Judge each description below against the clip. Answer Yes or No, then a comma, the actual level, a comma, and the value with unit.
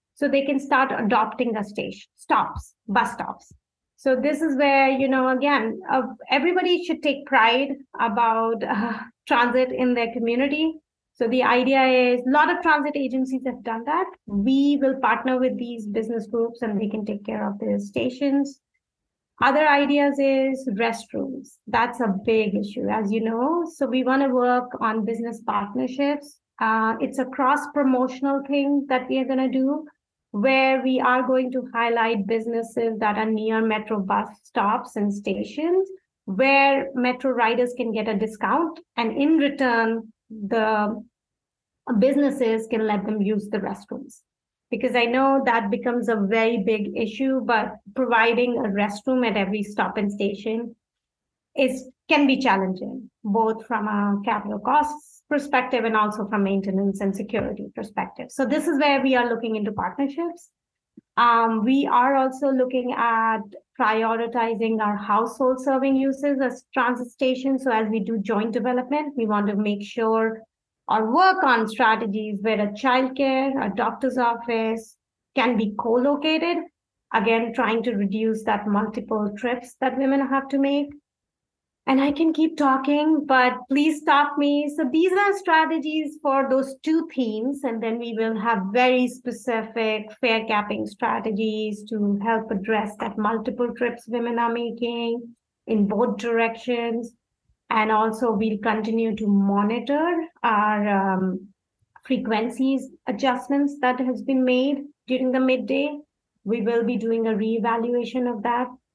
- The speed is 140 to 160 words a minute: Yes, average, 155 wpm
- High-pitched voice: Yes, high, 240 Hz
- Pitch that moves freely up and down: No, average, 3.3 semitones